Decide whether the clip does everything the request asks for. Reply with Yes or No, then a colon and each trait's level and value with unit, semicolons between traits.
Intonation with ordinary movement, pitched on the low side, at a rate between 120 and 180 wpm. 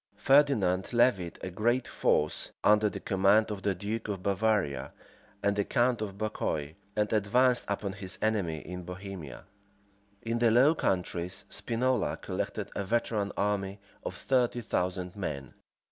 Yes: average, 3.7 semitones; low, 100 Hz; average, 145 wpm